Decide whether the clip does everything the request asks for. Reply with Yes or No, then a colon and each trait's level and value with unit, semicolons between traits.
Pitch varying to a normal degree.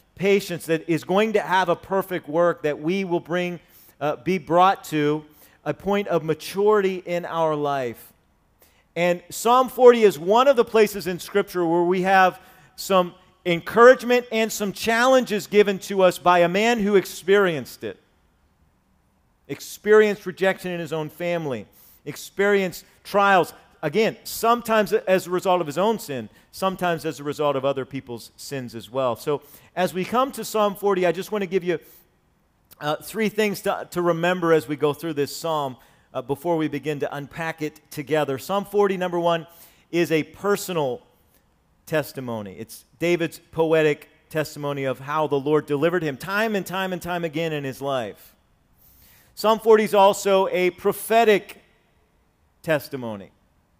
Yes: average, 4.9 semitones